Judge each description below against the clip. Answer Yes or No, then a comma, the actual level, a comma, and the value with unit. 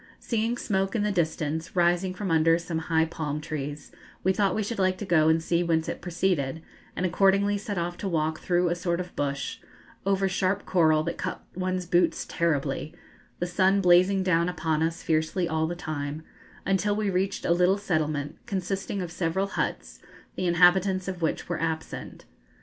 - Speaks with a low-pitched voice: No, medium, 175 Hz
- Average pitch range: Yes, average, 3.0 semitones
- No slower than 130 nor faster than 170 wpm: No, average, 185 wpm